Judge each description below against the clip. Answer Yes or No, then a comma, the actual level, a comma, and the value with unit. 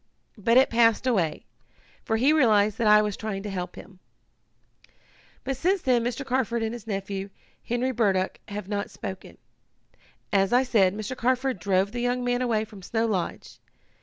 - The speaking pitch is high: Yes, high, 220 Hz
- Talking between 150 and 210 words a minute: Yes, average, 170 wpm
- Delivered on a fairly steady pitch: No, average, 3.6 semitones